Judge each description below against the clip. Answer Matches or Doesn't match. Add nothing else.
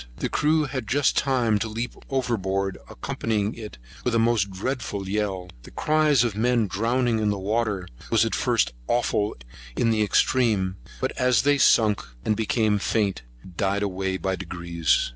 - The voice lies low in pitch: Matches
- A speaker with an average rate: Matches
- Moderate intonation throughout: Matches